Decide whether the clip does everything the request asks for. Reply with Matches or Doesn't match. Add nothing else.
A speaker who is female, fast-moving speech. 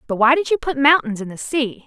Matches